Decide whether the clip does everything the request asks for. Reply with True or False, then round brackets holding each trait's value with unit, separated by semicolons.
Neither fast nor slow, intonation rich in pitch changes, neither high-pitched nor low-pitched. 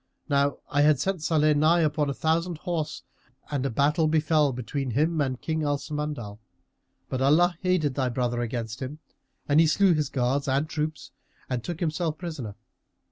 False (175 wpm; 3.1 semitones; 150 Hz)